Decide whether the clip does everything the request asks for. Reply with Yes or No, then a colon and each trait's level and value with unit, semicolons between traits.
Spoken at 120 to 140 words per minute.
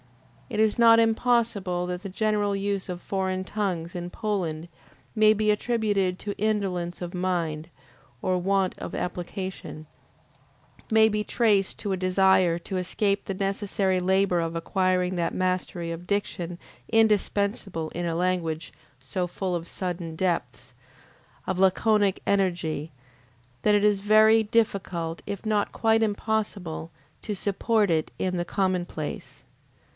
Yes: slow, 135 wpm